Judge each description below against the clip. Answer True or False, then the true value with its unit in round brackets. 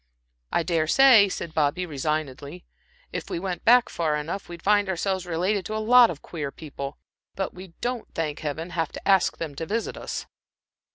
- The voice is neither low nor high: True (170 Hz)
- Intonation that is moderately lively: True (4.0 semitones)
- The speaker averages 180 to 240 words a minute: True (185 wpm)